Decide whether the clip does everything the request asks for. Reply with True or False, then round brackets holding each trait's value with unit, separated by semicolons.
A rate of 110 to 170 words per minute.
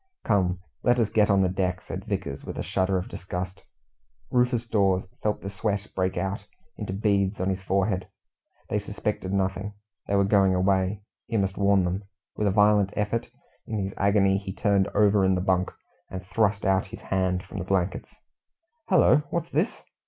False (180 wpm)